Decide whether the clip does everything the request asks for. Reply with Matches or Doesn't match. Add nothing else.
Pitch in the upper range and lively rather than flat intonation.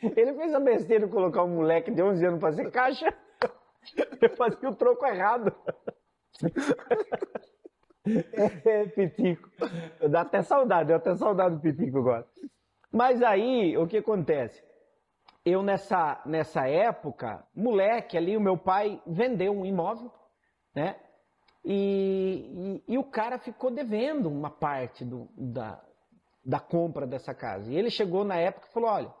Matches